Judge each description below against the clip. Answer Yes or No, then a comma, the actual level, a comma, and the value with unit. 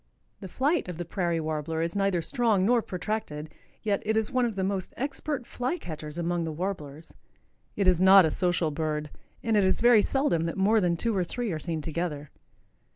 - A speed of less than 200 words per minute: No, fast, 205 wpm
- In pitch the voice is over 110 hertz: Yes, medium, 185 Hz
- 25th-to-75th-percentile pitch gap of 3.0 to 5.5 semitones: Yes, average, 5.1 semitones